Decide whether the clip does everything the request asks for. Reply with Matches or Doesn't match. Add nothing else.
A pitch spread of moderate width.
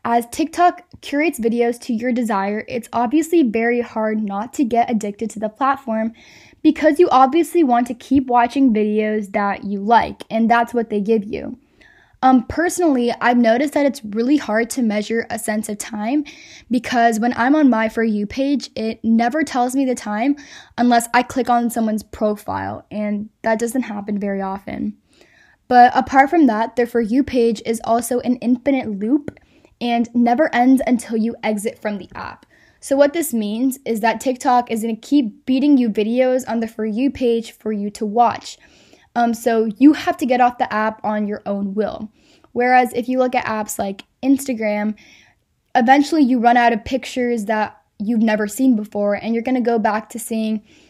Matches